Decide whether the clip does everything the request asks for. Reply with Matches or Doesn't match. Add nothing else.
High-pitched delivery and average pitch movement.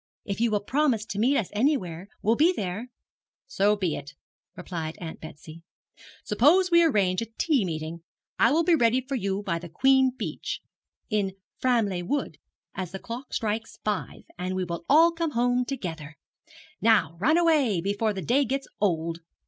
Doesn't match